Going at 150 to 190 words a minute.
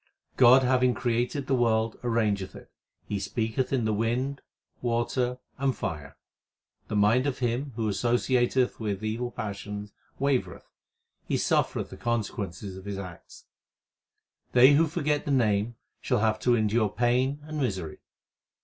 No: average, 140 wpm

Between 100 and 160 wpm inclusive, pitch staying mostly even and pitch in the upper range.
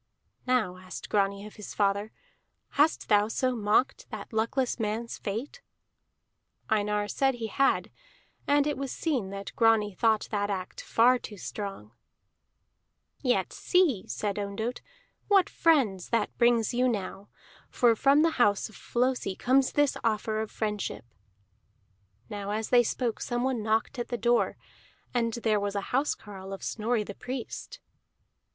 No: average, 145 wpm; average, 3.5 semitones; high, 225 Hz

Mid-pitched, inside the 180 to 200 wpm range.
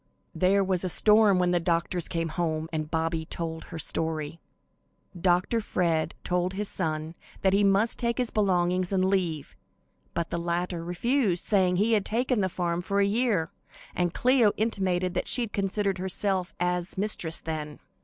No: medium, 180 Hz; average, 165 wpm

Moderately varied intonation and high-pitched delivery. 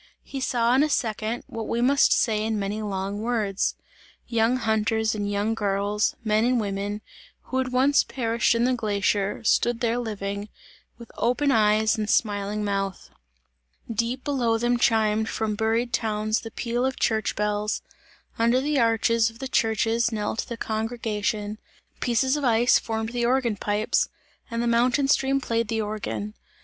No: narrow, 2.2 semitones; high, 225 Hz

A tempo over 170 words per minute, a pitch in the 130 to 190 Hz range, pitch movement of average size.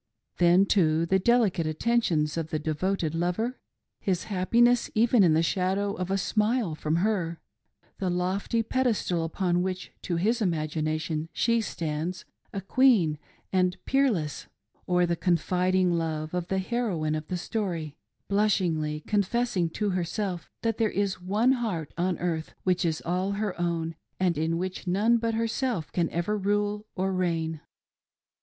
No: average, 165 wpm; medium, 185 Hz; average, 4.0 semitones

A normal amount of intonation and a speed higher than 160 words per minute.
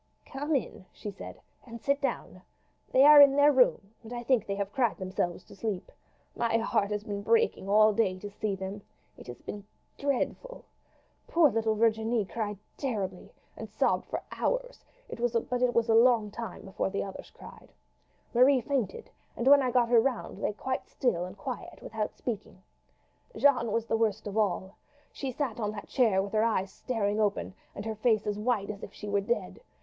Yes: average, 3.6 semitones; average, 185 wpm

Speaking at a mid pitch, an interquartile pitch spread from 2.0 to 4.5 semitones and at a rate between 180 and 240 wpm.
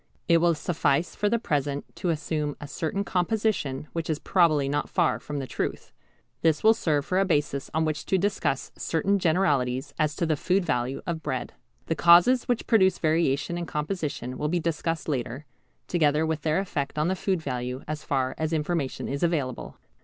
Yes: medium, 155 Hz; average, 3.4 semitones; average, 190 wpm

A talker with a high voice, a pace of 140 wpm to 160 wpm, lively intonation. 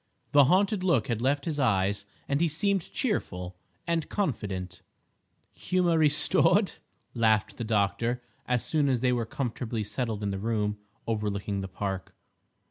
No: low, 115 Hz; average, 145 wpm; wide, 6.3 semitones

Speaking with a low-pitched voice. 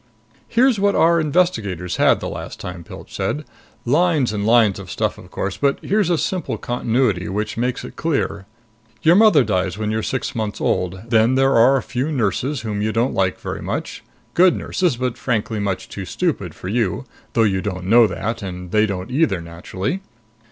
Yes: low, 115 Hz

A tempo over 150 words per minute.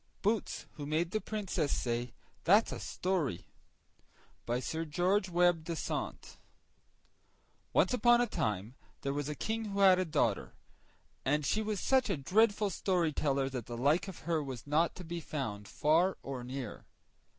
Yes: average, 160 wpm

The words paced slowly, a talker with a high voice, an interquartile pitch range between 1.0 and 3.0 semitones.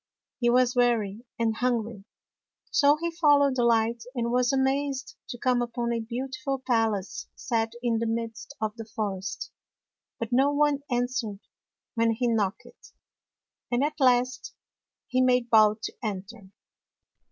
No: average, 145 wpm; high, 240 Hz; narrow, 2.4 semitones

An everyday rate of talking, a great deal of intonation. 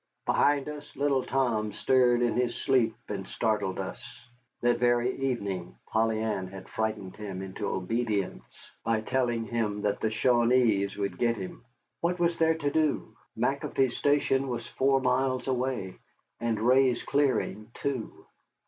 No: average, 145 wpm; average, 3.7 semitones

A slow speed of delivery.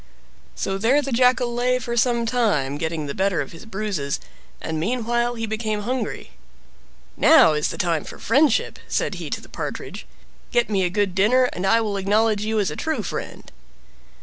No: average, 180 wpm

